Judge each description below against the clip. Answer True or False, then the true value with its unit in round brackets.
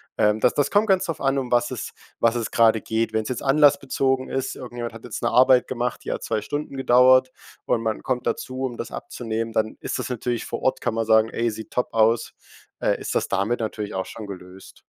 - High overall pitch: False (120 Hz)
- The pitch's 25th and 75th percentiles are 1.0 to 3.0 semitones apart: True (2.7 semitones)